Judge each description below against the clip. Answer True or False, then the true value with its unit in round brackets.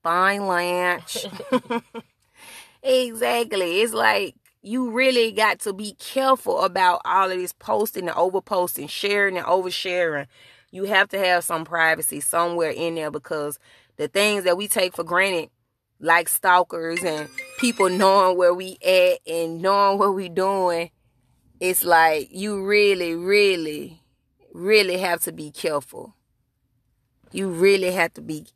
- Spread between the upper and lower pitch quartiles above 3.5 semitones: False (3.1 semitones)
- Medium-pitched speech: True (180 Hz)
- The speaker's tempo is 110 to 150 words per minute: True (140 wpm)